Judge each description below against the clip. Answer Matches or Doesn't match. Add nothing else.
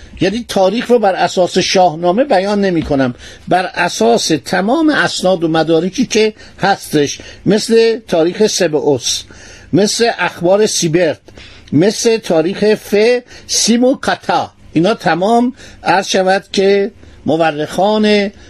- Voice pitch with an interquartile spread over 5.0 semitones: Doesn't match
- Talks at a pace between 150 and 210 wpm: Doesn't match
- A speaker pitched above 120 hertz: Matches